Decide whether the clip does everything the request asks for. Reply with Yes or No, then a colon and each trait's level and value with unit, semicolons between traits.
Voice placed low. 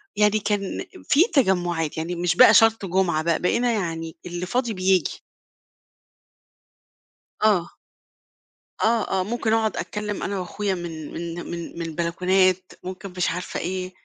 No: medium, 185 Hz